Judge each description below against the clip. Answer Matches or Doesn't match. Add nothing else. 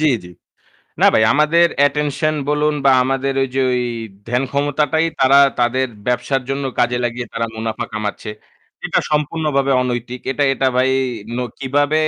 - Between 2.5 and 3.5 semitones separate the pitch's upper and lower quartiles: Matches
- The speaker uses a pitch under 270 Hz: Matches